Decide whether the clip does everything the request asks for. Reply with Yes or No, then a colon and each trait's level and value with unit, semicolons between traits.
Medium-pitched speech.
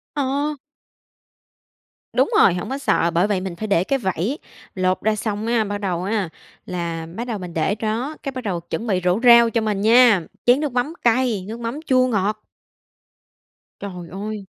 No: high, 215 Hz